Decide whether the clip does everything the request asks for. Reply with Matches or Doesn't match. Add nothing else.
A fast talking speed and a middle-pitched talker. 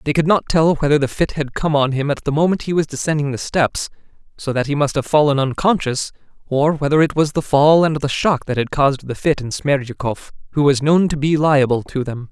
Matches